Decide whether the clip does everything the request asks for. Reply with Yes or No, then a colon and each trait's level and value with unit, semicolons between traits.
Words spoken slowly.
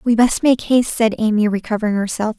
No: average, 200 wpm